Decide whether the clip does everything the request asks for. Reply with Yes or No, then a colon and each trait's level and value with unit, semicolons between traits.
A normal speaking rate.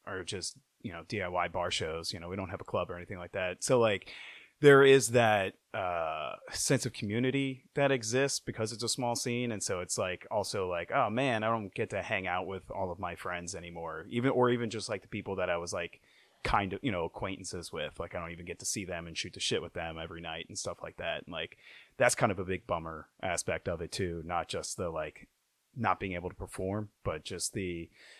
No: fast, 245 wpm